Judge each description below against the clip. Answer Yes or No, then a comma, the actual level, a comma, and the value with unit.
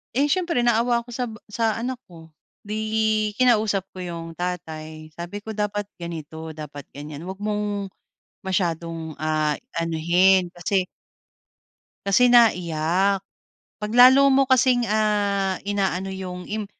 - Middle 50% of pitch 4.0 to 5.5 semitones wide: Yes, average, 4.7 semitones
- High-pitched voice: Yes, high, 195 Hz